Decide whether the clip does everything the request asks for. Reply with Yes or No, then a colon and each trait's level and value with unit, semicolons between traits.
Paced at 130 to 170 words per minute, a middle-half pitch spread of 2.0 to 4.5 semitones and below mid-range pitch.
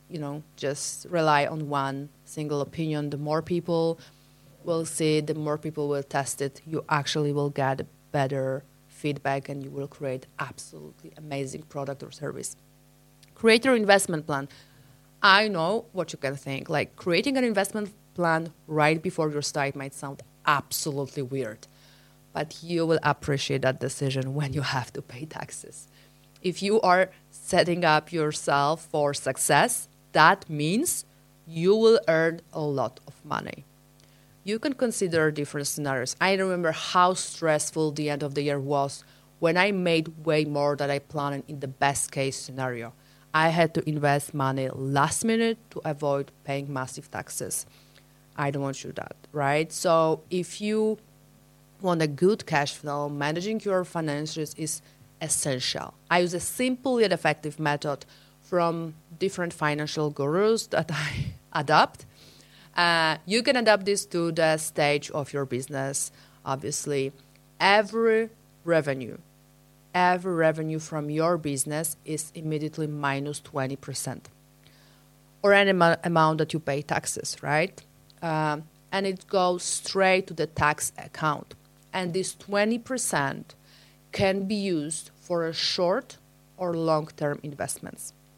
No: average, 145 wpm; average, 3.3 semitones; medium, 150 Hz